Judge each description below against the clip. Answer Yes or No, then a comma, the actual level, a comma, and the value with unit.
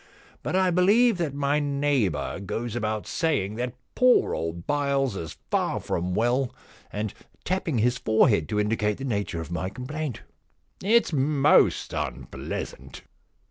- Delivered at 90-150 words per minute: Yes, average, 140 wpm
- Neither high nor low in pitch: No, low, 125 Hz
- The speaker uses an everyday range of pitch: No, wide, 6.0 semitones